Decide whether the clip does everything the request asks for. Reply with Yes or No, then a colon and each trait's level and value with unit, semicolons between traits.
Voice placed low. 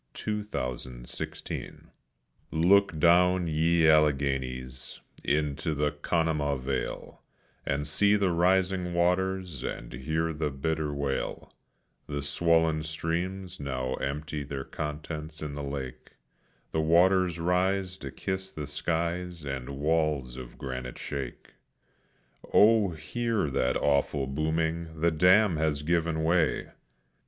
Yes: very low, 80 Hz